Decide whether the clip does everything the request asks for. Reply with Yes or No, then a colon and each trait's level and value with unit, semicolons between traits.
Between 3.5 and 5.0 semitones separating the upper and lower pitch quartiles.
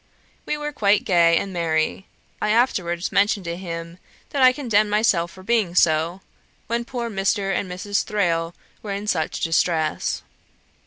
Yes: average, 3.9 semitones